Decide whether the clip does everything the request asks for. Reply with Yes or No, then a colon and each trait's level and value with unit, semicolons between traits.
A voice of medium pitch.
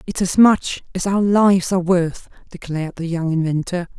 Yes: medium, 180 Hz